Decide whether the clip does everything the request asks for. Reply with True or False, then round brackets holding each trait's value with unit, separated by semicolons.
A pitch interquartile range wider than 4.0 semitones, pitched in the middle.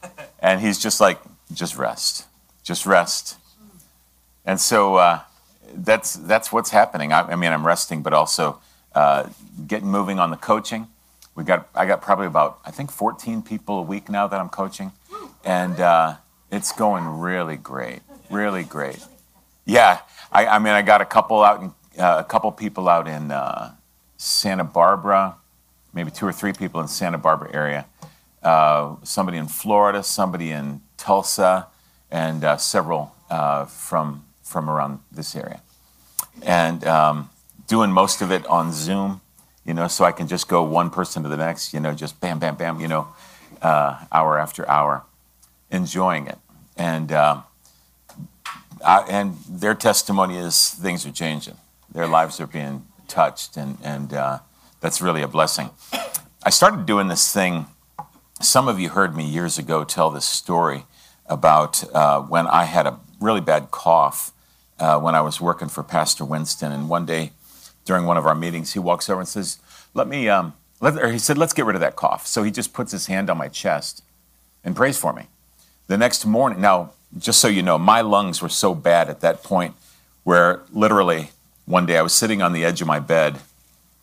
False (4.5 semitones; 80 Hz)